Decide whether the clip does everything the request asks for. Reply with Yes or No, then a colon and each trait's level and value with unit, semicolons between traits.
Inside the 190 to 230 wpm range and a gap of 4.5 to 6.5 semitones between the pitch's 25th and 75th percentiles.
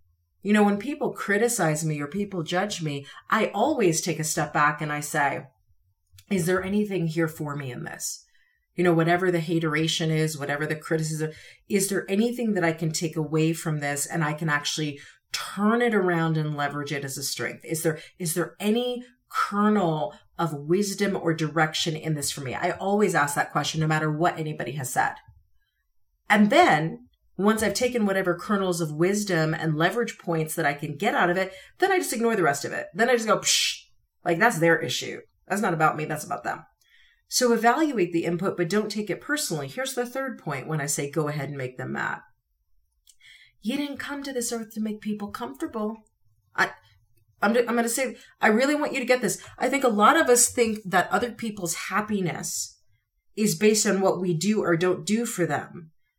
Yes: fast, 205 wpm; wide, 5.5 semitones